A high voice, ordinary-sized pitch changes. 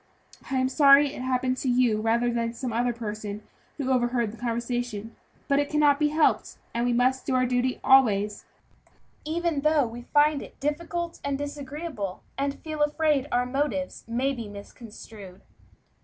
Yes: very high, 255 Hz; average, 3.6 semitones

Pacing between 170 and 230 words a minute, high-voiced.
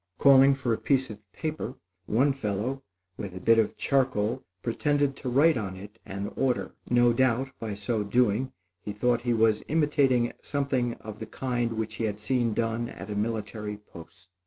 No: average, 180 wpm; low, 115 Hz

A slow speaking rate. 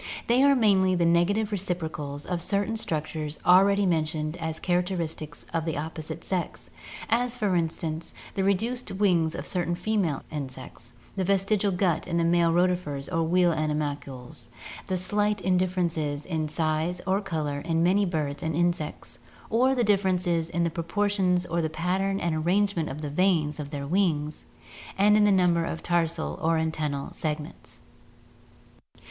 No: average, 160 wpm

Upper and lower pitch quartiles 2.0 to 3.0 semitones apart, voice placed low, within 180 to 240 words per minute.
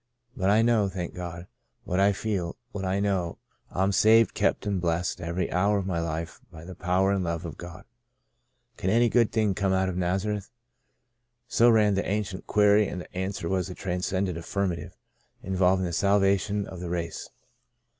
Yes: narrow, 2.4 semitones; very low, 95 Hz; average, 195 wpm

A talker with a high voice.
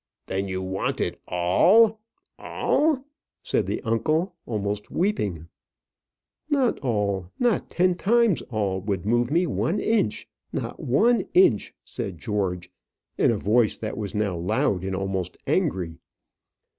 No: low, 105 Hz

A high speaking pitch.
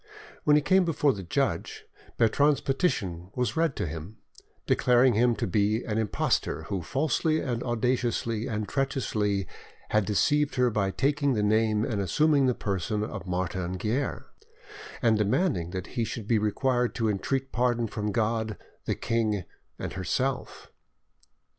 No: low, 115 Hz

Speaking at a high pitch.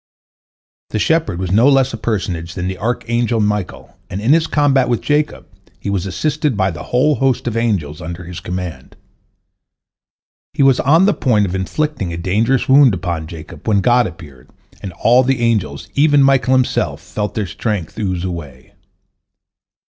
No: low, 110 Hz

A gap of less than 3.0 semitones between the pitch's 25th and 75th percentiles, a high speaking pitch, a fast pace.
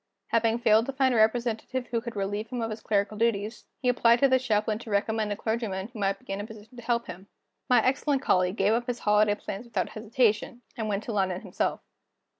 Yes: narrow, 2.5 semitones; high, 220 Hz; fast, 230 wpm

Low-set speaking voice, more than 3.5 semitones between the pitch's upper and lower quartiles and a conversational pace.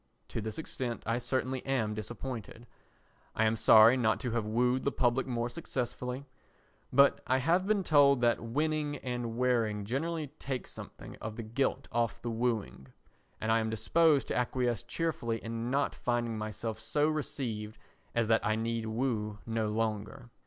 No: low, 120 Hz; average, 3.0 semitones; average, 165 wpm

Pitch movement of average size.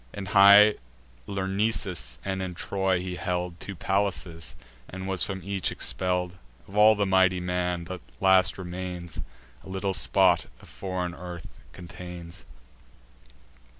No: narrow, 1.5 semitones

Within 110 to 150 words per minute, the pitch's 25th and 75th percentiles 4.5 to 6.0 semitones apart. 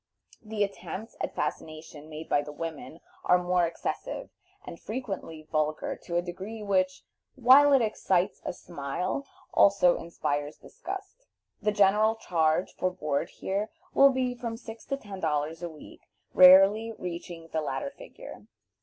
Yes: average, 145 wpm; average, 5.3 semitones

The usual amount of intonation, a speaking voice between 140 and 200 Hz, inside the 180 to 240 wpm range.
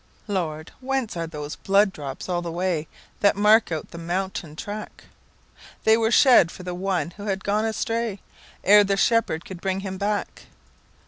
No: average, 3.7 semitones; high, 190 Hz; average, 150 wpm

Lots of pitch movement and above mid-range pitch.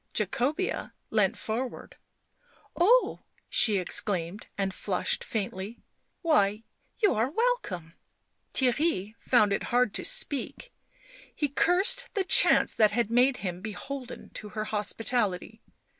Yes: wide, 6.0 semitones; high, 225 Hz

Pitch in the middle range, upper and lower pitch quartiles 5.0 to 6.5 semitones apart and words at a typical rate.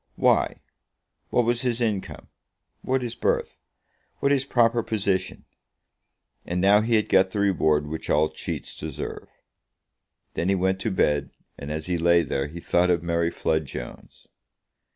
No: very low, 95 Hz; wide, 5.6 semitones; average, 155 wpm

